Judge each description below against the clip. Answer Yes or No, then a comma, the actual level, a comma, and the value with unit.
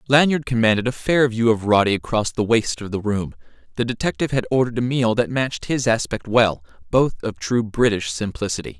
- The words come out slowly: No, average, 190 wpm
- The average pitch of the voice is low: Yes, low, 115 Hz